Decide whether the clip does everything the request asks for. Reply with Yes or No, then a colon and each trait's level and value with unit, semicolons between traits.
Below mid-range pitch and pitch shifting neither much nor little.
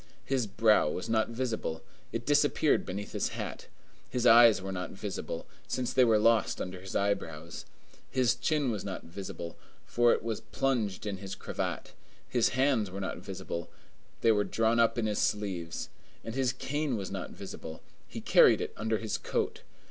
Yes: low, 110 Hz; average, 3.5 semitones